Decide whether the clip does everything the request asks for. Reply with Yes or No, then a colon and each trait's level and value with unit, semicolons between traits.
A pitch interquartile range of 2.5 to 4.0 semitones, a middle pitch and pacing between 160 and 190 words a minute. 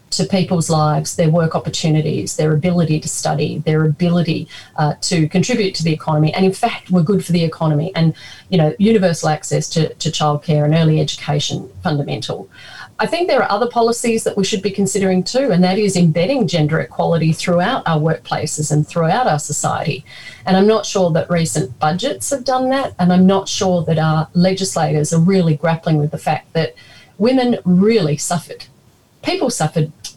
Yes: average, 3.6 semitones; medium, 165 Hz; average, 185 wpm